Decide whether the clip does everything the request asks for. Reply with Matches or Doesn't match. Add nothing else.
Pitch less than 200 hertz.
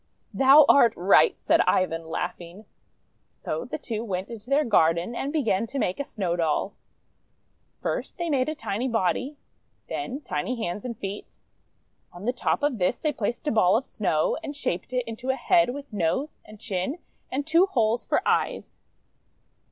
Doesn't match